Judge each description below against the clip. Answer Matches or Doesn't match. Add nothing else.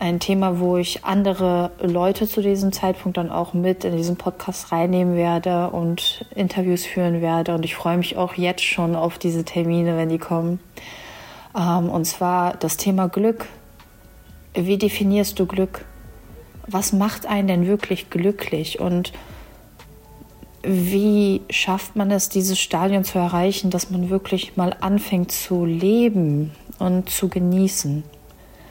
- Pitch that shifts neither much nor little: Doesn't match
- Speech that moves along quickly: Doesn't match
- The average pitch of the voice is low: Doesn't match